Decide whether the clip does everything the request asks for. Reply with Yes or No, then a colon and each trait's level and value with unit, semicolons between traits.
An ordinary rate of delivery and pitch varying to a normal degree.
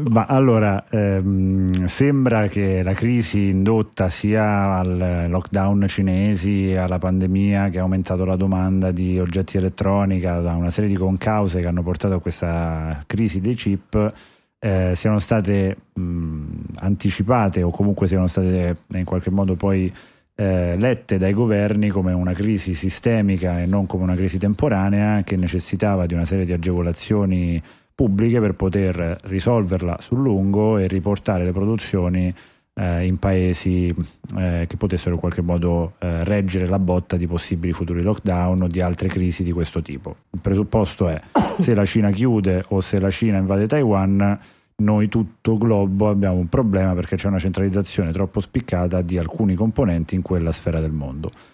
No: average, 160 wpm; narrow, 2.1 semitones